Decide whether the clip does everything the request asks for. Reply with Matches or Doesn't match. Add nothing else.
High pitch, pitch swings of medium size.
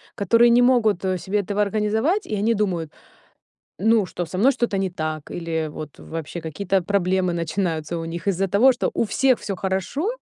Matches